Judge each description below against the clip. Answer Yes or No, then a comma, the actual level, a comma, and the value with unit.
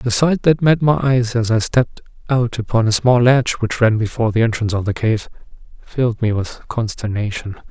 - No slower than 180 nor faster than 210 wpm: Yes, average, 200 wpm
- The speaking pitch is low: Yes, low, 115 Hz